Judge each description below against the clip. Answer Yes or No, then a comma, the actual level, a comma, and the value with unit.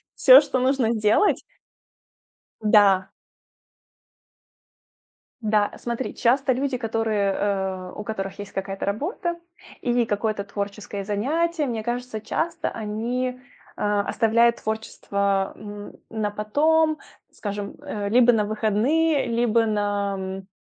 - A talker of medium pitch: No, high, 220 Hz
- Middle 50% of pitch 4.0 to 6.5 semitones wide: No, average, 3.6 semitones